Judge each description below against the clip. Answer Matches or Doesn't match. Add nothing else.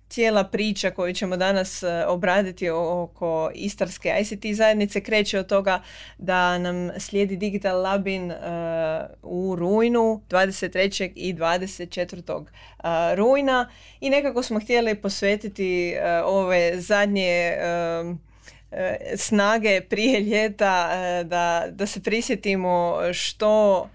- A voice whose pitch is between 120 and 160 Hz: Doesn't match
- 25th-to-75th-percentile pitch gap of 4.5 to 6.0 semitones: Doesn't match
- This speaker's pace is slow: Matches